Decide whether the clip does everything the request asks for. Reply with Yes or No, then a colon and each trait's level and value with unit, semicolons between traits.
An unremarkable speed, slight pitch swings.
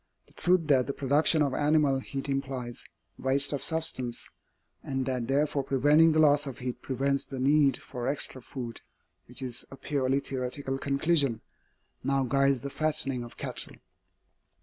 Yes: average, 155 wpm; narrow, 1.9 semitones